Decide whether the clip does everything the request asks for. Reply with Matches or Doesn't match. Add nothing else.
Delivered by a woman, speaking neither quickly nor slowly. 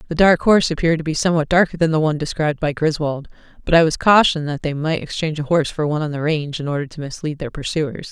Doesn't match